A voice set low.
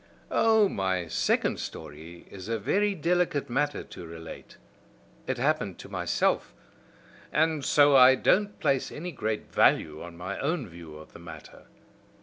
Yes: low, 125 Hz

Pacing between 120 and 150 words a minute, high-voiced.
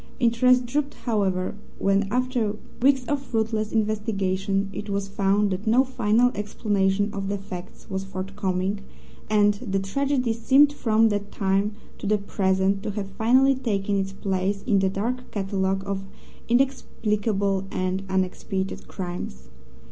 Yes: average, 140 wpm; high, 205 Hz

